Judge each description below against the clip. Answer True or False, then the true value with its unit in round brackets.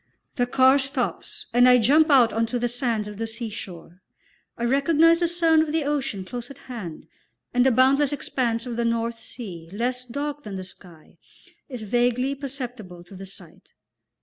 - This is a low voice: False (245 Hz)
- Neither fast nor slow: True (180 wpm)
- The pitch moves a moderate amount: True (3.7 semitones)